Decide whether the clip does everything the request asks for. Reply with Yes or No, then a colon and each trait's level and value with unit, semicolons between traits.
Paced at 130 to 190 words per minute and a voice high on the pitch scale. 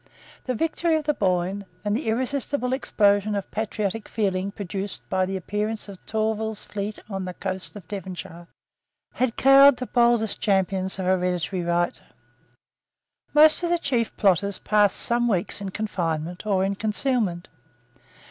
Yes: average, 150 wpm; high, 205 Hz